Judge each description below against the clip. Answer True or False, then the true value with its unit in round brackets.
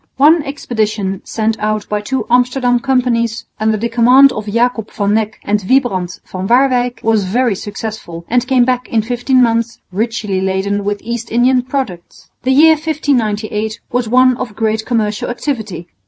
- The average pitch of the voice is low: False (230 Hz)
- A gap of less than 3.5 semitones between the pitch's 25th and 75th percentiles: True (3.1 semitones)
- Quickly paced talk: False (160 wpm)